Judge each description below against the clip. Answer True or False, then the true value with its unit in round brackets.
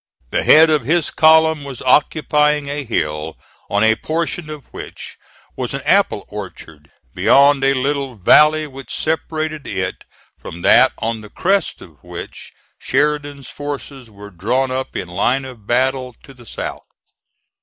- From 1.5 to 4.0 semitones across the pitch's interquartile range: False (4.9 semitones)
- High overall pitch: False (135 Hz)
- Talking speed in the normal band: True (150 wpm)